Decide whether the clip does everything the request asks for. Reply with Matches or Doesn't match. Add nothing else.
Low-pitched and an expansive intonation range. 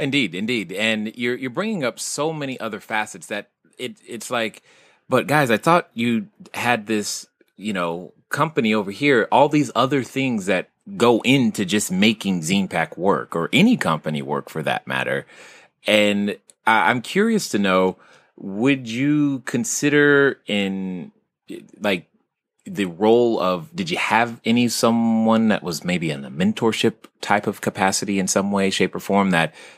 Matches